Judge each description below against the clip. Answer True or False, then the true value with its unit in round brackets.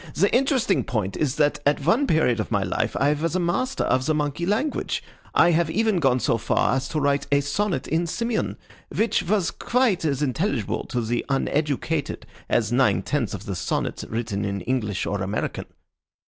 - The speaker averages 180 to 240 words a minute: True (185 wpm)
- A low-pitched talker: False (145 Hz)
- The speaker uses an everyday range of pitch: False (6.4 semitones)